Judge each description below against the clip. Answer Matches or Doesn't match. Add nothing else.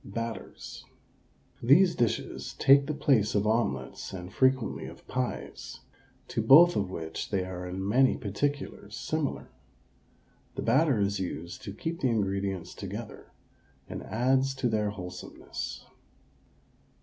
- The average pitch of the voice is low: Matches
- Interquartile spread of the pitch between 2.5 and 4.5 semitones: Doesn't match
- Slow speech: Matches